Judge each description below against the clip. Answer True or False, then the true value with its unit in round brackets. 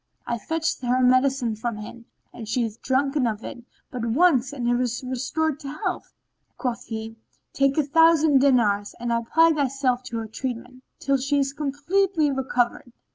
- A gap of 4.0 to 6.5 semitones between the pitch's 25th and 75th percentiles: False (3.2 semitones)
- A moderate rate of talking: True (165 wpm)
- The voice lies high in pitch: True (255 Hz)